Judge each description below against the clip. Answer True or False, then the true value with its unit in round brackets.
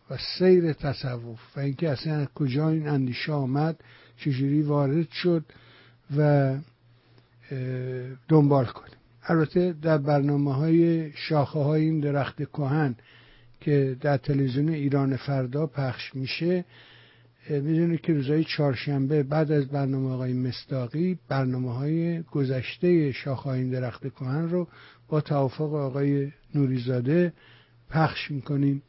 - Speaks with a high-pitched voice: False (140 Hz)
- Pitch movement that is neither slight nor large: True (3.1 semitones)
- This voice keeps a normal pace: False (115 wpm)